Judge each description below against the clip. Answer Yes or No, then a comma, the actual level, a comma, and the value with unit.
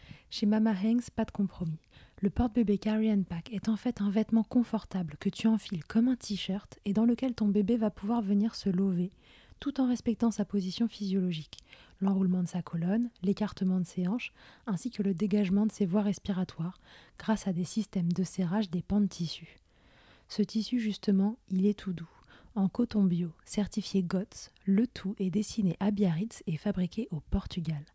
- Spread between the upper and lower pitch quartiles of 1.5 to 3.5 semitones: Yes, average, 2.9 semitones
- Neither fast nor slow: Yes, average, 185 wpm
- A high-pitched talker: Yes, high, 200 Hz